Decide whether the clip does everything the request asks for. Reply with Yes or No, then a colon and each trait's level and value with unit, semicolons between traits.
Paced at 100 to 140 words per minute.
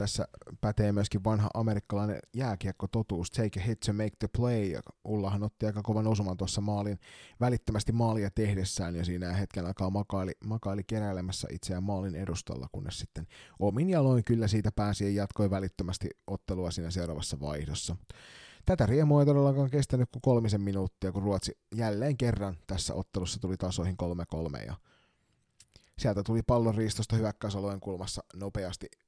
No: fast, 155 wpm